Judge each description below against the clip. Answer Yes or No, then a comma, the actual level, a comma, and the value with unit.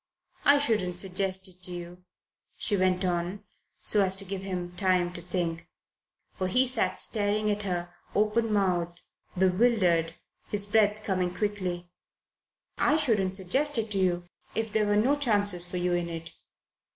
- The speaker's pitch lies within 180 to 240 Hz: Yes, high, 190 Hz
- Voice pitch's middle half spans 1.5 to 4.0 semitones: Yes, average, 3.0 semitones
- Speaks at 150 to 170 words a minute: Yes, average, 155 wpm